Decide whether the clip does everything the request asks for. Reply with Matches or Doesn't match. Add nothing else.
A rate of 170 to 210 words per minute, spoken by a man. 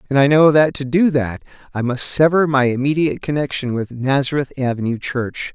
Matches